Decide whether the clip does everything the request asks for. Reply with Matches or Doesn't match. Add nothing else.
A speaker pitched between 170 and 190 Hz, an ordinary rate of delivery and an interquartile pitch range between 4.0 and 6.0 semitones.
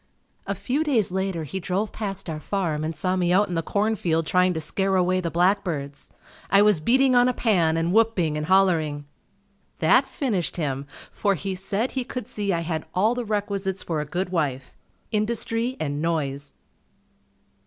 Matches